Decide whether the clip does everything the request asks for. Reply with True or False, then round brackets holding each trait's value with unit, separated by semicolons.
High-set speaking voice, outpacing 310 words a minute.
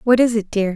True (220 Hz; 320 wpm)